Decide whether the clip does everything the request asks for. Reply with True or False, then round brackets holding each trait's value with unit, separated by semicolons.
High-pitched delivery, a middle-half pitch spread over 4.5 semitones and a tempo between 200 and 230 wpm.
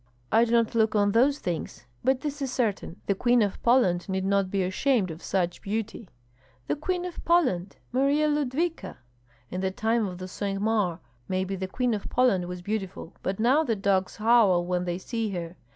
False (210 Hz; 5.0 semitones; 190 wpm)